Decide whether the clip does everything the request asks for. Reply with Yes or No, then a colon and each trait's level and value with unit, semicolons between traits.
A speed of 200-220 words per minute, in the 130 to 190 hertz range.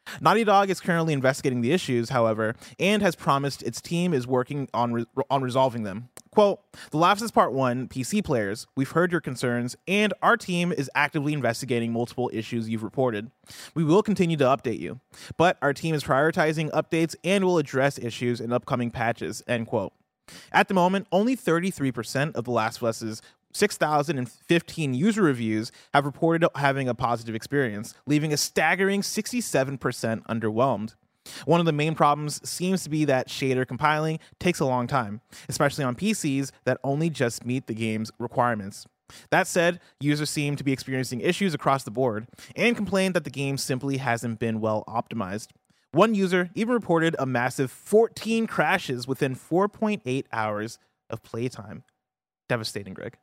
No: average, 165 wpm; medium, 140 Hz